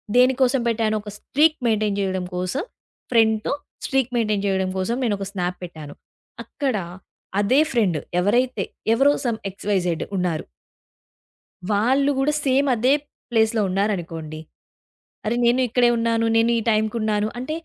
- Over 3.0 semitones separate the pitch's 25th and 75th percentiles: Yes, average, 4.1 semitones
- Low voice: No, high, 220 Hz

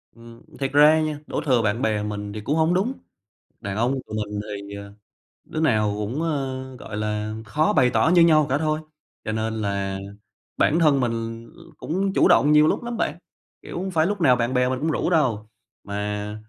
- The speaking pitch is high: No, low, 125 Hz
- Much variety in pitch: Yes, wide, 6.5 semitones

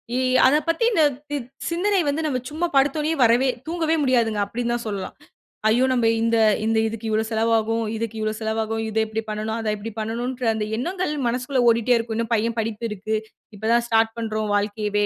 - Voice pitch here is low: No, high, 230 Hz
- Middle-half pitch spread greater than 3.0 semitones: No, average, 2.7 semitones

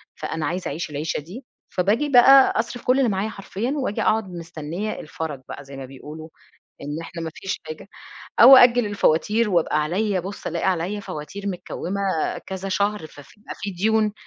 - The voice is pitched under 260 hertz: Yes, high, 190 Hz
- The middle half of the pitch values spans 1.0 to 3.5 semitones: No, average, 5.1 semitones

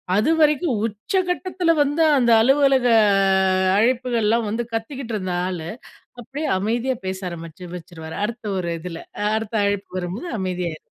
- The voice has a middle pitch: No, high, 225 Hz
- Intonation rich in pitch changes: Yes, wide, 6.5 semitones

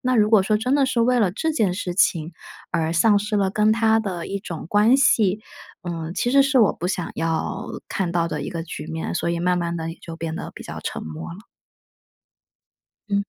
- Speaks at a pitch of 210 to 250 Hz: No, high, 190 Hz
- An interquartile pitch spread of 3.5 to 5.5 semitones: Yes, average, 4.6 semitones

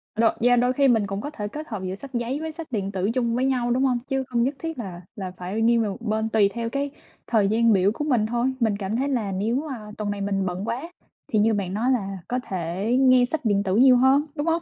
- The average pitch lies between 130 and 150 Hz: No, high, 230 Hz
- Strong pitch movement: No, average, 4.4 semitones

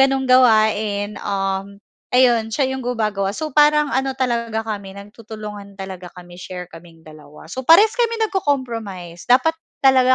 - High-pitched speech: Yes, high, 220 Hz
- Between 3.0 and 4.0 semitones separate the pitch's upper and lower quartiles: No, average, 5.1 semitones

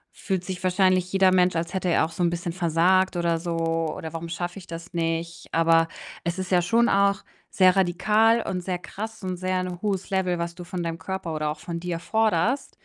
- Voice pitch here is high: No, medium, 180 Hz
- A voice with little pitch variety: Yes, narrow, 2.0 semitones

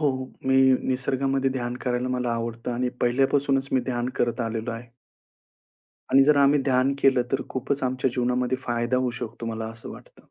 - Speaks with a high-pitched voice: No, low, 125 Hz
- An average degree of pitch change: No, narrow, 1.9 semitones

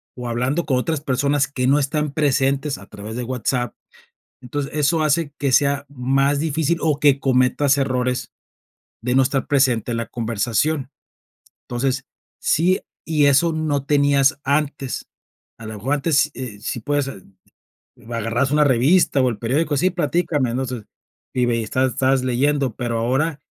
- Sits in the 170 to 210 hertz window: No, low, 135 Hz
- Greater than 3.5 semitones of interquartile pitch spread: No, average, 2.7 semitones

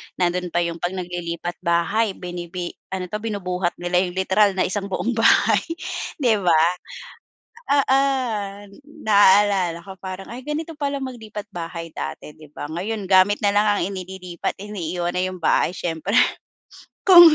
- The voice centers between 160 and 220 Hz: Yes, high, 190 Hz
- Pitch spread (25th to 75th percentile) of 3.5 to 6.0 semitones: No, average, 3.1 semitones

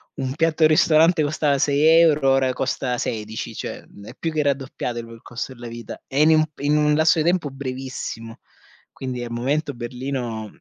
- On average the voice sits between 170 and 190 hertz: No, low, 135 Hz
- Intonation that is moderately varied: Yes, average, 4.0 semitones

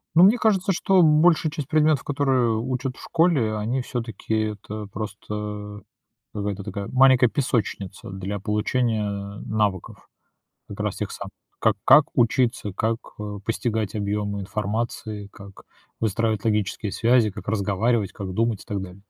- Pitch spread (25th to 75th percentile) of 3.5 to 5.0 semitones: Yes, average, 3.8 semitones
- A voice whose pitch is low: Yes, low, 110 Hz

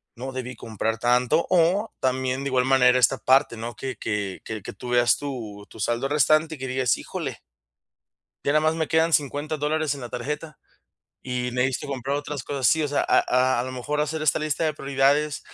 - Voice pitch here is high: No, low, 135 Hz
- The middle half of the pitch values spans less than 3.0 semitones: No, average, 3.3 semitones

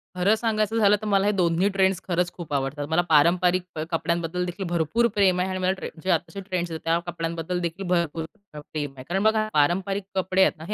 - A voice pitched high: No, medium, 180 Hz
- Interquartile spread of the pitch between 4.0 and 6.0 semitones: No, average, 2.8 semitones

